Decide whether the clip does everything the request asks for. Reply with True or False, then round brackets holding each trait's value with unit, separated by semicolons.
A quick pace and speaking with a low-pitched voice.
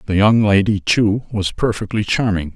False (165 wpm; 105 Hz)